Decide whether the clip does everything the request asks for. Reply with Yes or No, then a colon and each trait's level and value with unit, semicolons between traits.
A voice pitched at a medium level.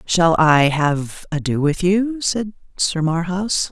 Yes: medium, 175 Hz